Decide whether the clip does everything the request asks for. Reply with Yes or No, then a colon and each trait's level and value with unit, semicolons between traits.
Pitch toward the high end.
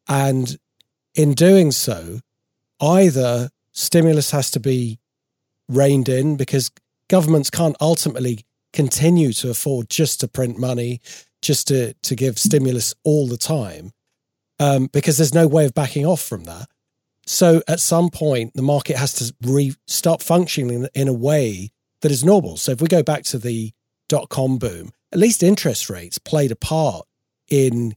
No: low, 135 Hz